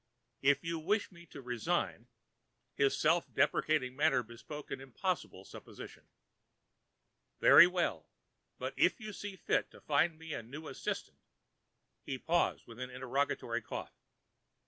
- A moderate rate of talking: No, slow, 125 wpm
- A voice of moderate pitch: Yes, medium, 150 Hz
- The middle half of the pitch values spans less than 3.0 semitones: No, average, 5.0 semitones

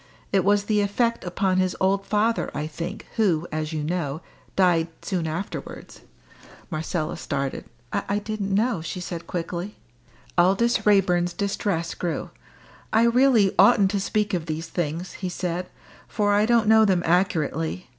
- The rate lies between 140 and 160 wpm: Yes, average, 155 wpm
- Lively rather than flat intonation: No, average, 3.5 semitones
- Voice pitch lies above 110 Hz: Yes, medium, 185 Hz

